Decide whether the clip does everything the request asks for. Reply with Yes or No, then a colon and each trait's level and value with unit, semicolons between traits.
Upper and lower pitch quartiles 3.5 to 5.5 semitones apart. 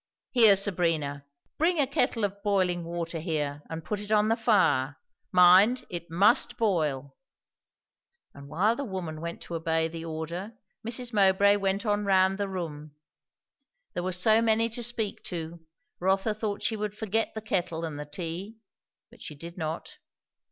Yes: average, 4.6 semitones